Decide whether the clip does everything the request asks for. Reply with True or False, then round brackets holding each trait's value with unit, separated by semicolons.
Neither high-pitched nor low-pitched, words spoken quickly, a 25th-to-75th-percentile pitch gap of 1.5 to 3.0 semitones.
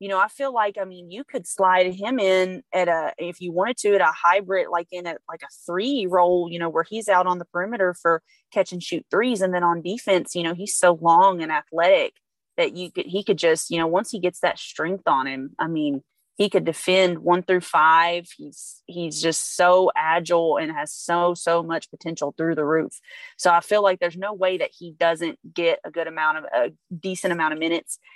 True (175 Hz; 230 wpm; 2.4 semitones)